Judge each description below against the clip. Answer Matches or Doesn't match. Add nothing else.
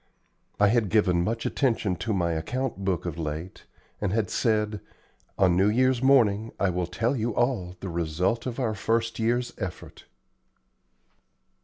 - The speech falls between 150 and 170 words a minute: Matches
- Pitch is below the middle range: Matches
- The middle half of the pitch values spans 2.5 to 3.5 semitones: Doesn't match